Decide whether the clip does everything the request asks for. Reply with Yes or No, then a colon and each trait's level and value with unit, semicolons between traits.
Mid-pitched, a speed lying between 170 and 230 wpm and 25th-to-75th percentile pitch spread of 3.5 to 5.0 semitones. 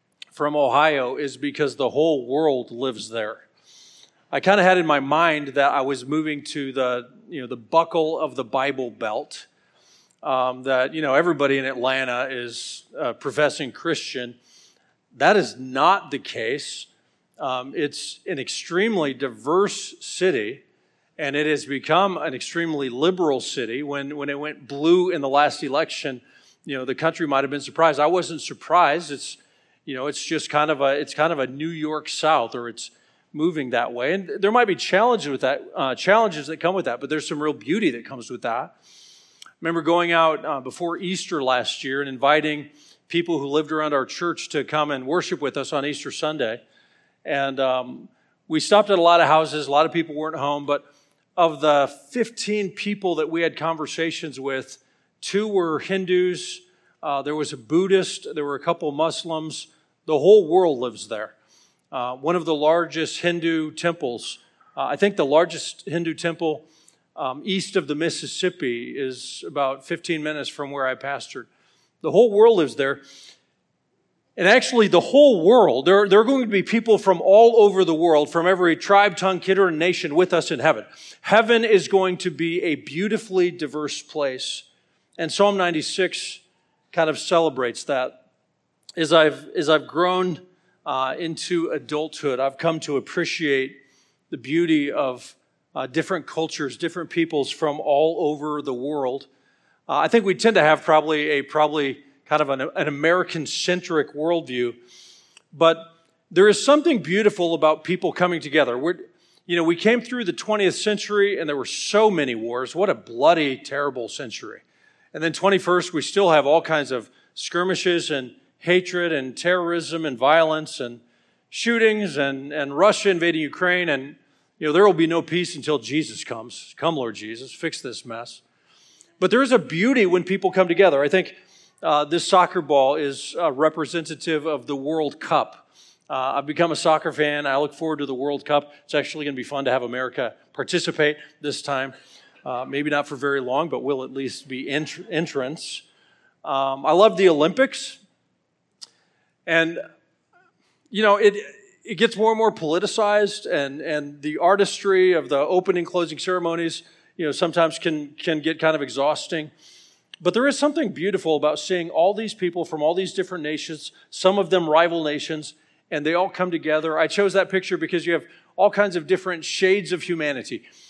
Yes: medium, 160 Hz; average, 180 wpm; average, 4.0 semitones